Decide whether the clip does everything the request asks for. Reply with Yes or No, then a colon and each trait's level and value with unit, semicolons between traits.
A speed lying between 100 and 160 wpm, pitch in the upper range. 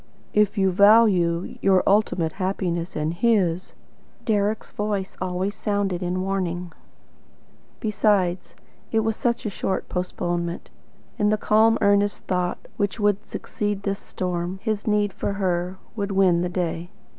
Yes: slow, 135 wpm; high, 195 Hz